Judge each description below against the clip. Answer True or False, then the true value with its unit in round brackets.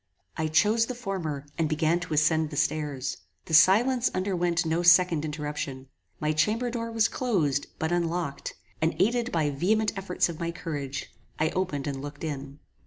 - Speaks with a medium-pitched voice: True (160 Hz)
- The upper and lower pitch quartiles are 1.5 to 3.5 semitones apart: False (4.2 semitones)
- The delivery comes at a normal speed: True (170 wpm)